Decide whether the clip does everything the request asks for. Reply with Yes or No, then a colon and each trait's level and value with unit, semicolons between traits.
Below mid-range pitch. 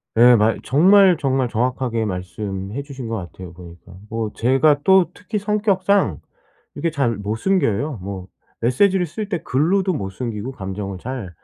Yes: low, 125 Hz